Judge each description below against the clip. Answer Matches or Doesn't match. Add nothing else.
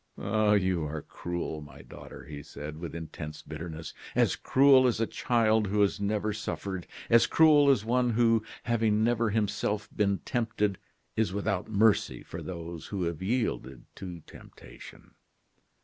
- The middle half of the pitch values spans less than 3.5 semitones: Doesn't match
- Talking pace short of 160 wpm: Matches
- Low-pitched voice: Matches